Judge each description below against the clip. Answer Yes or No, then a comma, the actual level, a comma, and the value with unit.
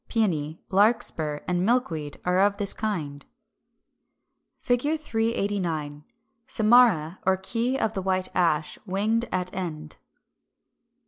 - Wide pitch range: Yes, wide, 5.8 semitones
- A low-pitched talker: No, high, 190 Hz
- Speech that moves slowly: Yes, slow, 120 wpm